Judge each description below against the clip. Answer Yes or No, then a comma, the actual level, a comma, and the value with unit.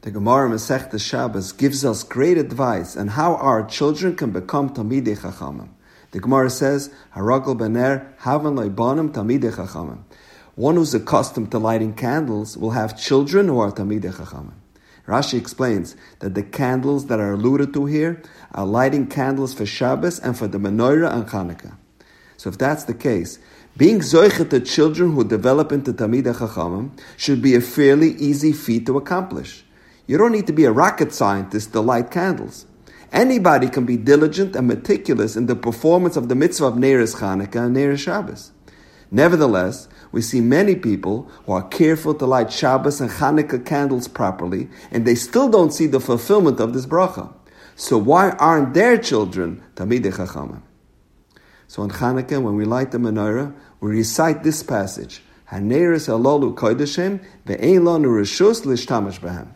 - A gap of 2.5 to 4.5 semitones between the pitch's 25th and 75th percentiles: No, average, 5.1 semitones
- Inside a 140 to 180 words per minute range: Yes, average, 150 wpm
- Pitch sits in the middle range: No, low, 130 Hz